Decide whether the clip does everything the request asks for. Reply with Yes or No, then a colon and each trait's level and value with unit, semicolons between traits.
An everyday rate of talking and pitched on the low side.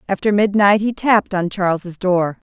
No: average, 165 wpm; high, 195 Hz